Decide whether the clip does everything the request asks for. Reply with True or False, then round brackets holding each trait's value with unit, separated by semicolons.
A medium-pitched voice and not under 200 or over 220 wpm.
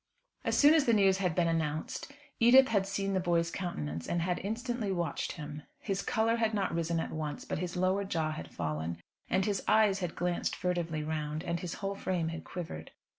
True (180 Hz; 205 wpm)